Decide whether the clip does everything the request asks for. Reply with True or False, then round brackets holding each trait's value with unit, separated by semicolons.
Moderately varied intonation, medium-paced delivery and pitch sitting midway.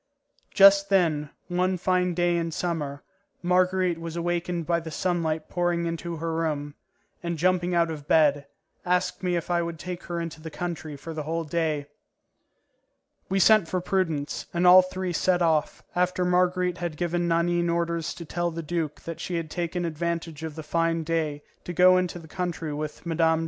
False (1.7 semitones; 180 wpm; 170 Hz)